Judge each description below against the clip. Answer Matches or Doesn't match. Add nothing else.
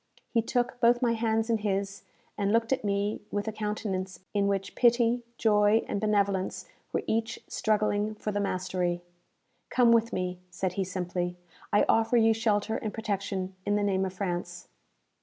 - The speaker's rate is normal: Matches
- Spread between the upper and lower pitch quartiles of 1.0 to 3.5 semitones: Matches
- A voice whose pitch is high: Matches